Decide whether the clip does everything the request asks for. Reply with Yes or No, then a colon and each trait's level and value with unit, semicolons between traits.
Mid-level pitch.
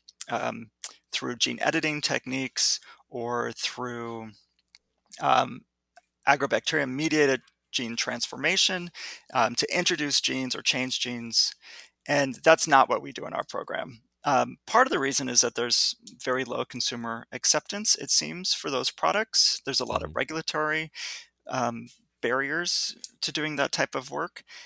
No: low, 130 Hz